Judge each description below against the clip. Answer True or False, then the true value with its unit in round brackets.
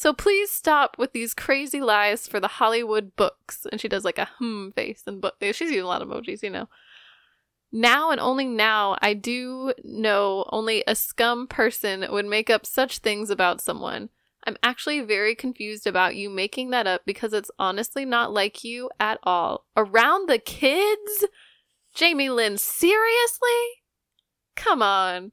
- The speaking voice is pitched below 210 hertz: False (235 Hz)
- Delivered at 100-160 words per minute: False (170 wpm)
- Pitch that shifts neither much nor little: True (4.7 semitones)